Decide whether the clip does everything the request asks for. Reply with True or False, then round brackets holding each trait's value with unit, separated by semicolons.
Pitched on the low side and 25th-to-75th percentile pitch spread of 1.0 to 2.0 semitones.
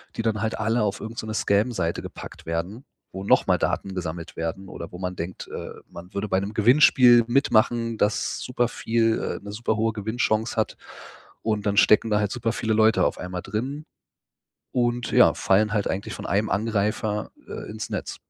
False (110 Hz; 2.7 semitones)